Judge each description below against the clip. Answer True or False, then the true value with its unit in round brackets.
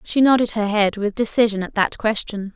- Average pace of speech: False (210 wpm)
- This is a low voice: False (215 Hz)